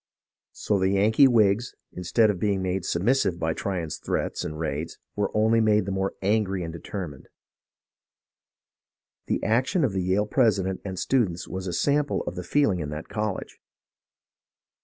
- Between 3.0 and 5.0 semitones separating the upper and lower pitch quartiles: Yes, average, 3.3 semitones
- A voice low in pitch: Yes, very low, 95 Hz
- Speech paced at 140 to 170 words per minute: Yes, average, 165 wpm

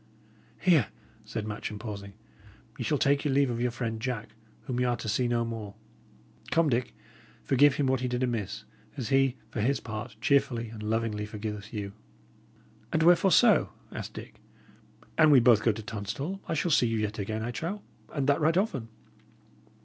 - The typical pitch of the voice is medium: No, low, 120 Hz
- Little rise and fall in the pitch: No, average, 4.4 semitones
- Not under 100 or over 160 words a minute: No, average, 185 wpm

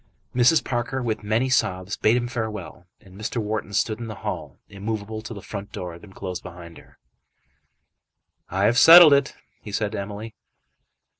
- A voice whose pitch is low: Yes, low, 110 Hz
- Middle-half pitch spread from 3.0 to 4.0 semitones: Yes, average, 3.4 semitones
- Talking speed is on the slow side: No, average, 175 wpm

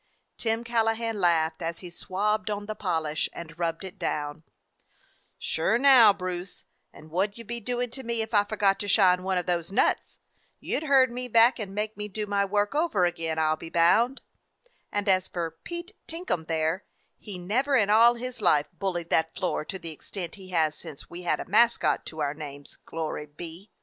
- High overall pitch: Yes, high, 195 Hz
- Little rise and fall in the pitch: No, average, 5.1 semitones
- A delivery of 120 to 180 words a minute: No, average, 200 wpm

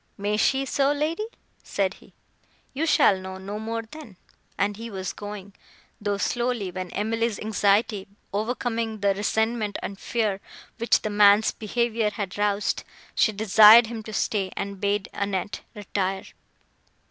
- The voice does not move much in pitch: Yes, narrow, 2.3 semitones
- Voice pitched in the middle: No, high, 210 Hz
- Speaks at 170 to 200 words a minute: No, average, 145 wpm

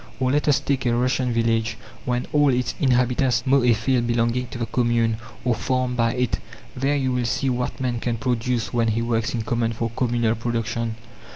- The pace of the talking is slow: No, average, 200 wpm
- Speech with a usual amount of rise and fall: No, narrow, 1.6 semitones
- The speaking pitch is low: Yes, low, 120 Hz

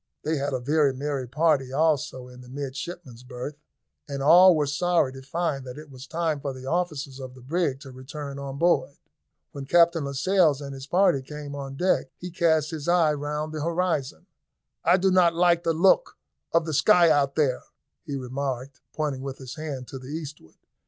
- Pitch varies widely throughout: No, average, 3.7 semitones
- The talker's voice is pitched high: No, medium, 145 Hz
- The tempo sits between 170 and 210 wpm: Yes, average, 195 wpm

